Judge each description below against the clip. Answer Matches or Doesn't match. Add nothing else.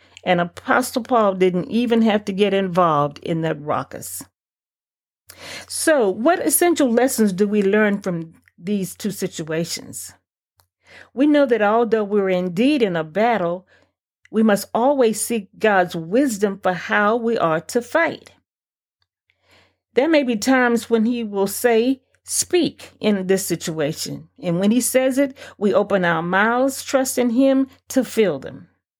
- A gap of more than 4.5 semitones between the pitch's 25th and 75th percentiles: Matches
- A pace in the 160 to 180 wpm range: Doesn't match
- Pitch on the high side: Matches